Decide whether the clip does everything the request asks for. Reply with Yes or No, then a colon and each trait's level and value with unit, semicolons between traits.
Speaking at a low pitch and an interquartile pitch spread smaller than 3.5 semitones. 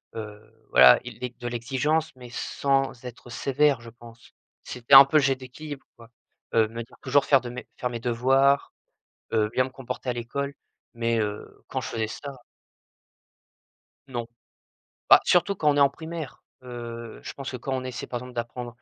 Yes: low, 125 Hz; average, 2.7 semitones